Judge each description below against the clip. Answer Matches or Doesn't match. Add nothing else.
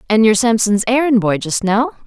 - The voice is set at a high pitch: Matches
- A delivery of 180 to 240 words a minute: Matches